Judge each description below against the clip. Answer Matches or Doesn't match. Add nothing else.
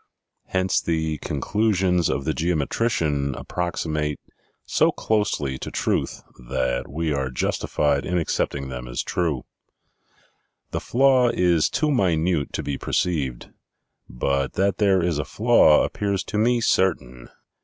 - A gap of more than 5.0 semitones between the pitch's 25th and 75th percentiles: Matches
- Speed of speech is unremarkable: Doesn't match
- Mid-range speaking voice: Doesn't match